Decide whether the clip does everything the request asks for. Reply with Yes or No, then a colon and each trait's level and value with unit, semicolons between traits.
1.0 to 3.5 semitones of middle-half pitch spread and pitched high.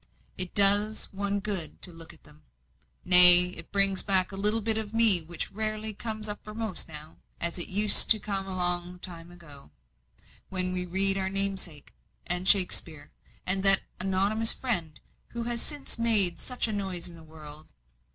Yes: average, 3.2 semitones; high, 195 Hz